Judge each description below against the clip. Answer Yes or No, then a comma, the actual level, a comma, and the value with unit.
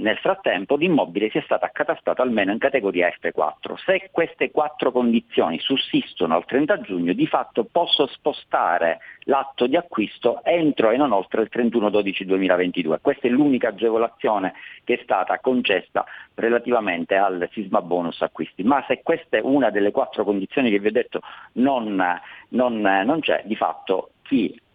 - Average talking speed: Yes, average, 160 wpm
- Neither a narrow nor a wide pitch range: No, wide, 5.7 semitones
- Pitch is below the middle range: Yes, low, 115 Hz